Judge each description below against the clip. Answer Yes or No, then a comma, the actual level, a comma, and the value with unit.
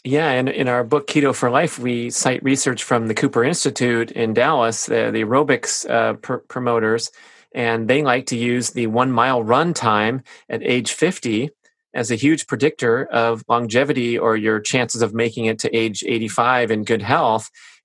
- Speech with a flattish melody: No, average, 3.1 semitones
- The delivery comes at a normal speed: Yes, average, 180 wpm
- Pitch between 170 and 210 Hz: No, low, 120 Hz